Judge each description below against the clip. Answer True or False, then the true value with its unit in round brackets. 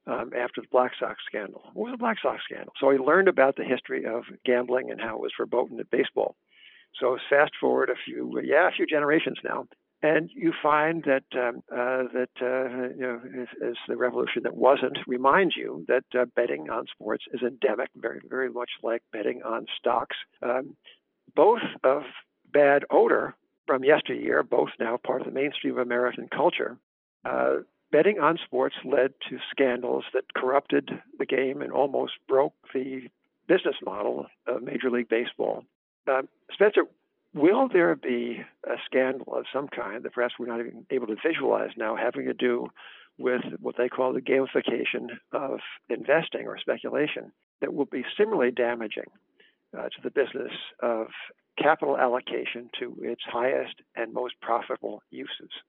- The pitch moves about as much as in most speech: False (2.0 semitones)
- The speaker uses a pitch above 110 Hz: True (125 Hz)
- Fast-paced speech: False (170 wpm)